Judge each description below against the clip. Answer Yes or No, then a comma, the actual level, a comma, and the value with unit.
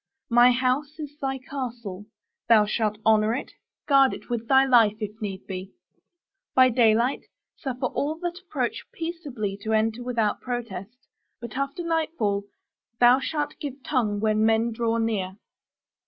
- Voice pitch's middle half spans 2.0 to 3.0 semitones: No, average, 3.9 semitones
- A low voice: No, high, 240 Hz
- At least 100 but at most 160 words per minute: Yes, average, 145 wpm